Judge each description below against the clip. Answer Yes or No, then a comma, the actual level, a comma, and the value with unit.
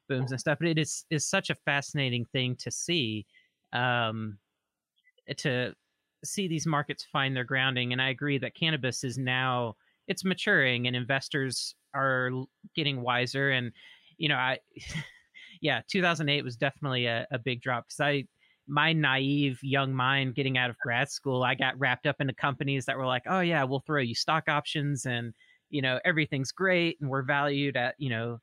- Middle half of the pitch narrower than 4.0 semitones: Yes, average, 2.8 semitones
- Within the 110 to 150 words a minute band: No, average, 180 wpm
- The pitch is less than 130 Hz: No, low, 135 Hz